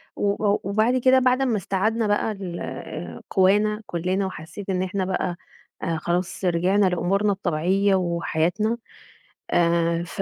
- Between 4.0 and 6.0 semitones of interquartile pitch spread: No, average, 3.0 semitones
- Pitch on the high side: Yes, high, 195 Hz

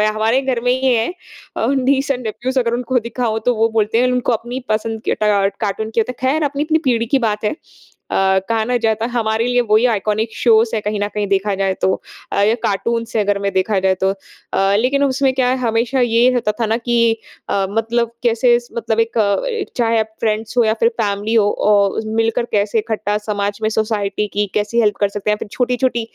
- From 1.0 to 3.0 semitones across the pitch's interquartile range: Yes, average, 2.7 semitones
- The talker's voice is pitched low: No, high, 225 Hz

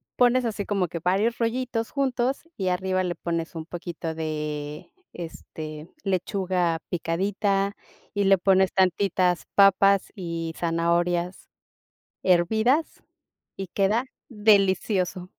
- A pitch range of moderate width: Yes, average, 3.1 semitones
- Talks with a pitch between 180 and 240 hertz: Yes, medium, 185 Hz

